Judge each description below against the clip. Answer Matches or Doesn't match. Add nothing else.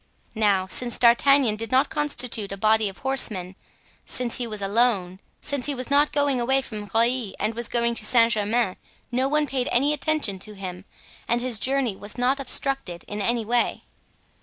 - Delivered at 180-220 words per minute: Matches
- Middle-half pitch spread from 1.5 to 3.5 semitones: Doesn't match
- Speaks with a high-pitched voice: Matches